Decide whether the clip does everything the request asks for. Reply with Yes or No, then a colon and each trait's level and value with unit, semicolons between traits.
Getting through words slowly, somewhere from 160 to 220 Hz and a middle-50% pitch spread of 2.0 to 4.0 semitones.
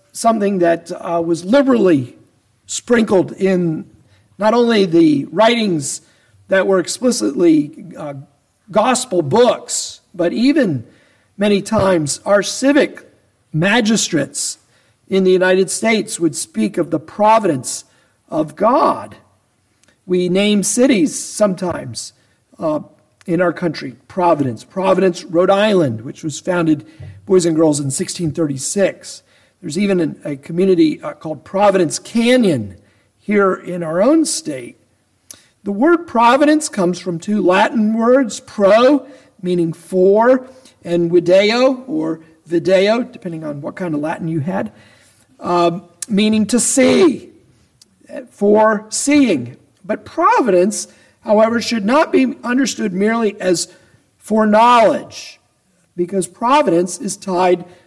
No: slow, 115 wpm; high, 190 Hz; wide, 5.6 semitones